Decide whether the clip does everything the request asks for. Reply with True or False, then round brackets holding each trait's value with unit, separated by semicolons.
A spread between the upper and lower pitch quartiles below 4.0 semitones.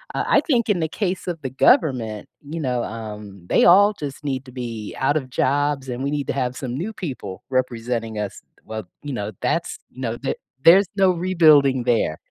False (5.5 semitones)